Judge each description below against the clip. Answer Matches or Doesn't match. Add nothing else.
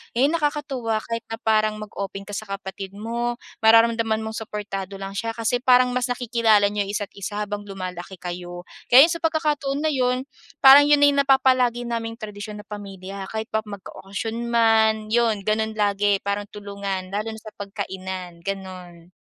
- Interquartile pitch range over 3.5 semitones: Doesn't match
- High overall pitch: Matches